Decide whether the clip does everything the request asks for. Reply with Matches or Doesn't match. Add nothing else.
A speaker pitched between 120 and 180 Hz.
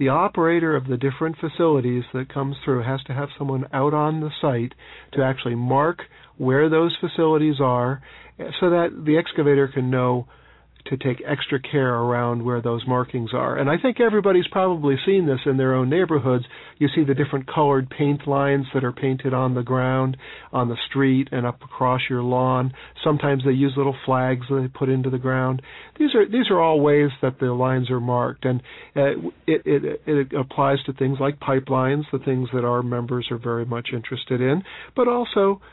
Matches